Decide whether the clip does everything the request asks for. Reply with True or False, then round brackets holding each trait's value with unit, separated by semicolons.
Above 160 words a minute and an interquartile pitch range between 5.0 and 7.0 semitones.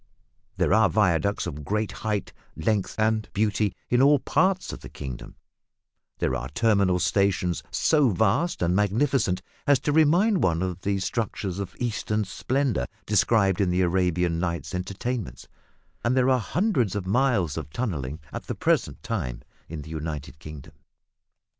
False (155 wpm; 5.5 semitones)